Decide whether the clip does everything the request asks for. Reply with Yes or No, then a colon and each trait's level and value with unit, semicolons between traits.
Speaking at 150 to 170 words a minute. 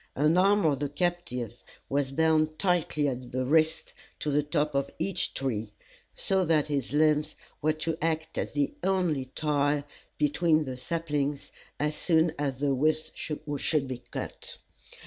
Yes: average, 155 wpm